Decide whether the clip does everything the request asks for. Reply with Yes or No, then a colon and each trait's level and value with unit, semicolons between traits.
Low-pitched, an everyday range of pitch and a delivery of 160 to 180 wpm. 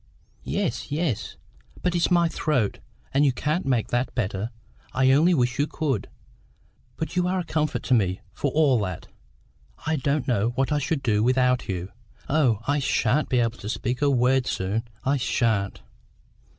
Yes: low, 130 Hz; average, 4.4 semitones; average, 175 wpm